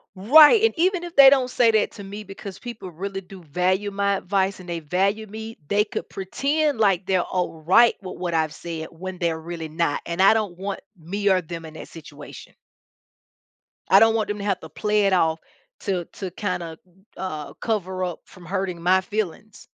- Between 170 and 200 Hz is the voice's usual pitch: Yes, high, 190 Hz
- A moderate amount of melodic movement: Yes, average, 3.3 semitones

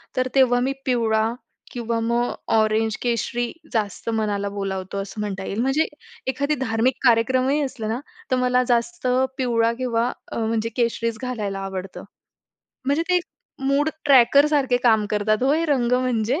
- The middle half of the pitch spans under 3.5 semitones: Yes, average, 2.8 semitones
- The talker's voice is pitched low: No, high, 235 Hz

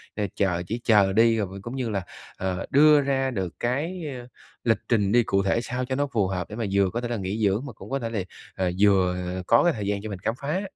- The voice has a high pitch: No, low, 110 Hz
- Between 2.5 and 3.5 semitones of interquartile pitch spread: No, average, 4.4 semitones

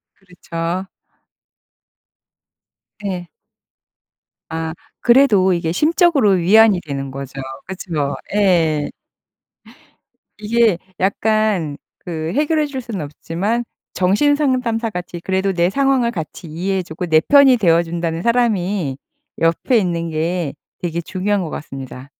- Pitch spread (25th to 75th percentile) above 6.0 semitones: No, average, 5.2 semitones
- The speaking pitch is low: No, medium, 185 Hz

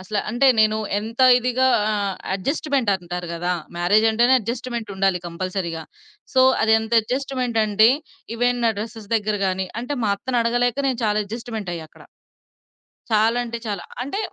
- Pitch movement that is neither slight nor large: Yes, average, 3.6 semitones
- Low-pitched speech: No, high, 220 Hz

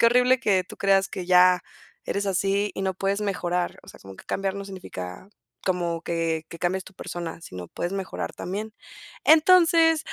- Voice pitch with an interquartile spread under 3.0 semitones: Yes, narrow, 2.6 semitones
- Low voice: No, high, 190 Hz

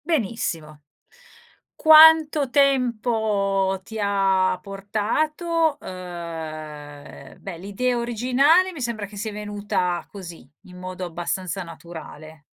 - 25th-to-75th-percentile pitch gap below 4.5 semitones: No, wide, 6.0 semitones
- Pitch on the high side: Yes, high, 200 Hz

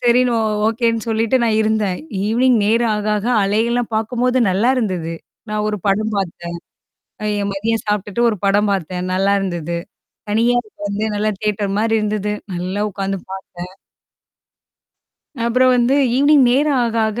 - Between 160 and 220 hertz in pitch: Yes, high, 215 Hz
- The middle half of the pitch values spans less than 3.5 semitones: Yes, average, 3.1 semitones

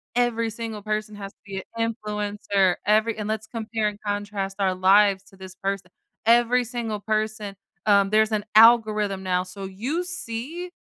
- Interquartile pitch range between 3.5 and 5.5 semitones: No, narrow, 2.4 semitones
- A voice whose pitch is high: Yes, high, 215 Hz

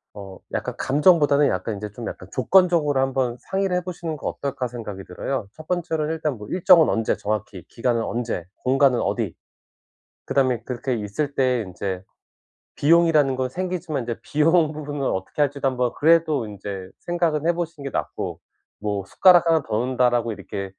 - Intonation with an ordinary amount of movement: No, wide, 5.8 semitones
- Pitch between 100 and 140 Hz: Yes, low, 135 Hz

